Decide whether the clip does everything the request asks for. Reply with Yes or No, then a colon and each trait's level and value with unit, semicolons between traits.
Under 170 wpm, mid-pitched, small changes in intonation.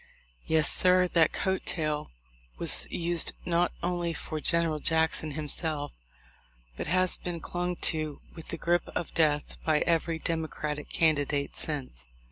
Yes: average, 140 wpm; medium, 160 Hz; narrow, 2.2 semitones